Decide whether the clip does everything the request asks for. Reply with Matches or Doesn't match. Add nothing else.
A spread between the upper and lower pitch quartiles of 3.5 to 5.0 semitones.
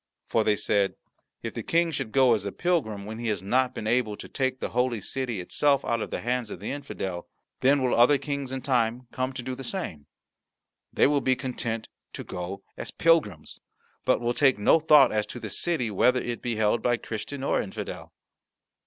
Matches